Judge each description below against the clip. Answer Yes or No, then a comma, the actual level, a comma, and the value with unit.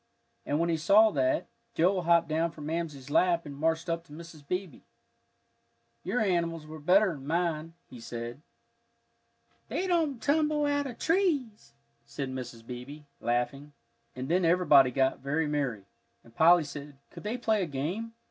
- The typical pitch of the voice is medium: Yes, medium, 165 Hz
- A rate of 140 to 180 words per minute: Yes, average, 155 wpm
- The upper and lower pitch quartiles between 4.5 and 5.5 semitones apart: Yes, average, 5.0 semitones